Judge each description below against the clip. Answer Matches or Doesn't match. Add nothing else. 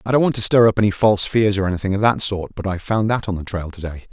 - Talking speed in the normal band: Doesn't match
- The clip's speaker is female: Doesn't match